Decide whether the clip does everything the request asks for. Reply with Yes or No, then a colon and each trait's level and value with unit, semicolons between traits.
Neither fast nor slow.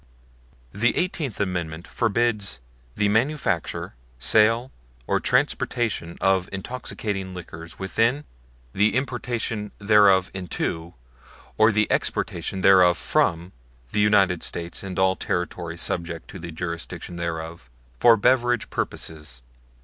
No: slow, 110 wpm